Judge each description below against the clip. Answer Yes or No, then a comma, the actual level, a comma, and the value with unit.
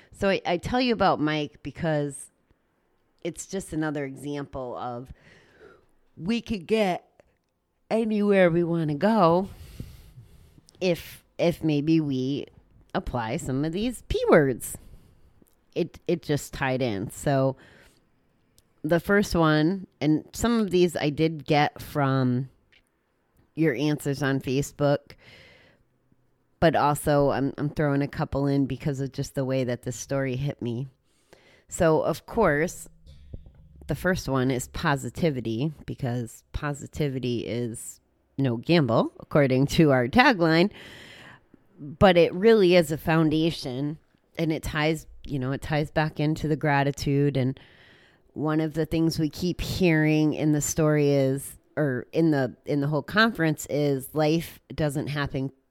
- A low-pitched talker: No, medium, 150 Hz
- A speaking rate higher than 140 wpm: No, slow, 135 wpm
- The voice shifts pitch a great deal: No, average, 3.4 semitones